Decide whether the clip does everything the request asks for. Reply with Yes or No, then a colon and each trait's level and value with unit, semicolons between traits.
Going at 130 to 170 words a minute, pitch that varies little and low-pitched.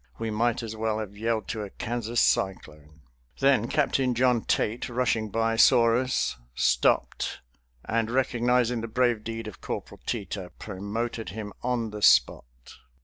Yes: average, 145 wpm; narrow, 2.2 semitones; low, 115 Hz